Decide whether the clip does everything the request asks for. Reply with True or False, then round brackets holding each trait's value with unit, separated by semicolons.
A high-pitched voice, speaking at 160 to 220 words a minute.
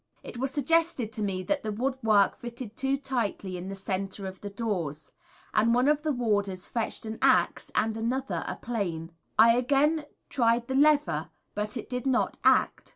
True (230 Hz; 180 wpm)